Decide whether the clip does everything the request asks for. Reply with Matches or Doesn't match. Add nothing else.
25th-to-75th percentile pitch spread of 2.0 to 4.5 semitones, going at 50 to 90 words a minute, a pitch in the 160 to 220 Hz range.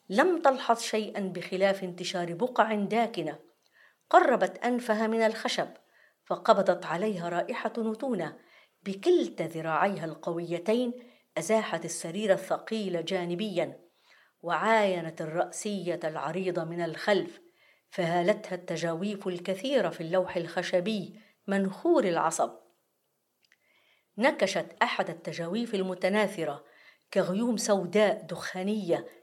Matches